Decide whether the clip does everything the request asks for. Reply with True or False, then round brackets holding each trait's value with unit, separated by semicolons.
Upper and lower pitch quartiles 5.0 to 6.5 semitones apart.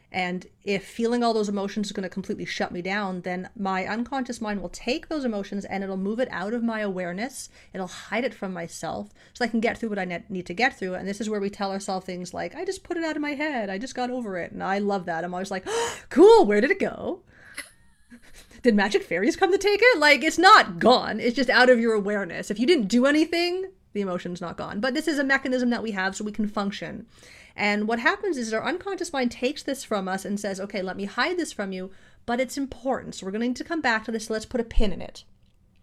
True (5.3 semitones)